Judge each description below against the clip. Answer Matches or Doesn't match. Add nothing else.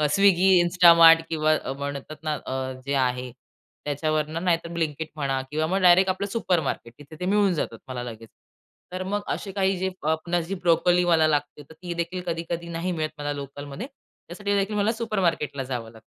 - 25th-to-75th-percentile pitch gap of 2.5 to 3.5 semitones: Doesn't match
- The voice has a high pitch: Doesn't match